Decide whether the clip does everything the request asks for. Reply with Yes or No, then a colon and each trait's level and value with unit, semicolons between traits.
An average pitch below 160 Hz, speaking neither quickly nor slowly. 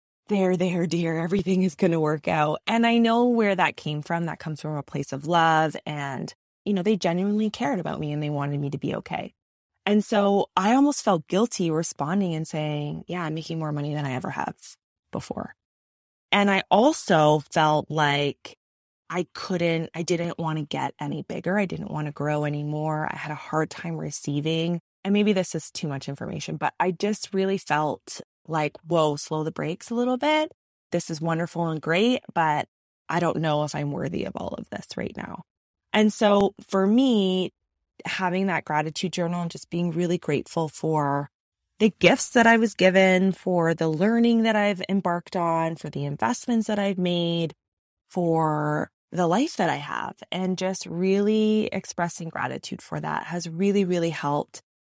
No: medium, 170 Hz; average, 185 wpm